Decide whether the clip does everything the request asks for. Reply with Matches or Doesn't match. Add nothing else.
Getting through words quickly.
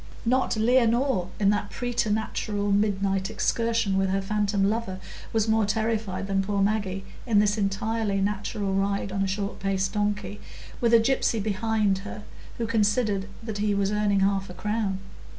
Doesn't match